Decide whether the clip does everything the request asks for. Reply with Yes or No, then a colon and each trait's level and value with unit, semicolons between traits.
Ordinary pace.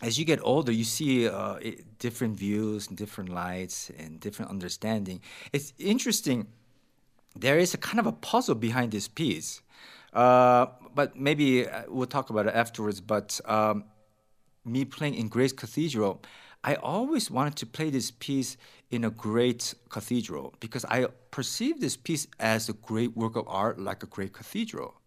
Yes: average, 165 wpm